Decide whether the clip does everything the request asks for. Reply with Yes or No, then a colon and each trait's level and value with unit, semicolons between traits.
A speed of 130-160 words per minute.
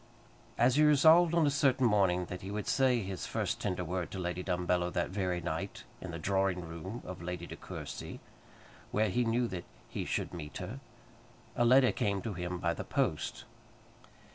No: average, 190 wpm